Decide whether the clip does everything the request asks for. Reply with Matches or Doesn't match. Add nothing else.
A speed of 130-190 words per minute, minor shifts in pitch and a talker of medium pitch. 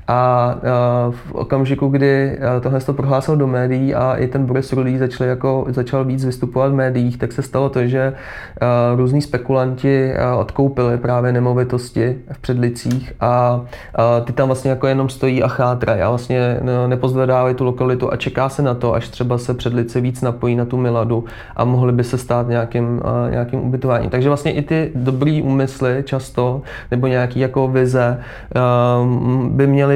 Doesn't match